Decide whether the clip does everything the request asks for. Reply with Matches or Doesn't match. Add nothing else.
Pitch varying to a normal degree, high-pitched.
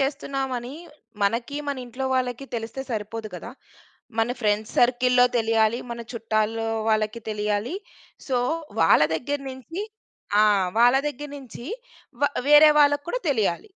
Matches